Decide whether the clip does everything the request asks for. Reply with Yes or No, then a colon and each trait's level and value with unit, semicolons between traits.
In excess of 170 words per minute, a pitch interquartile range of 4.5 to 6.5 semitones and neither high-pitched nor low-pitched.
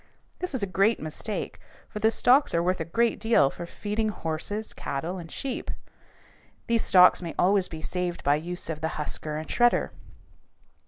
Yes: average, 180 wpm; average, 5.2 semitones; medium, 180 Hz